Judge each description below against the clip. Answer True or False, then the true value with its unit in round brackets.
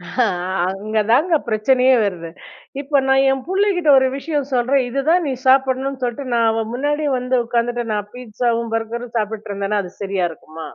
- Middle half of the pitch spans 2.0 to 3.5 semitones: False (4.0 semitones)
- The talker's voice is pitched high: True (245 Hz)